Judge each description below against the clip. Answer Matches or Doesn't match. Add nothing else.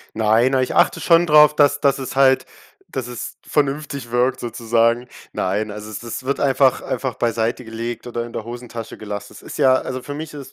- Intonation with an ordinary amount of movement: Matches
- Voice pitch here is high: Doesn't match